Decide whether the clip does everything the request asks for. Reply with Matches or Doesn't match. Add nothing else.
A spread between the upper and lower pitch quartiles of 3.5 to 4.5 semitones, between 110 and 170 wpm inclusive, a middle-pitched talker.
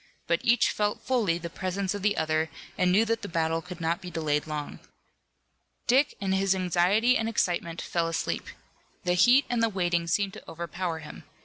Doesn't match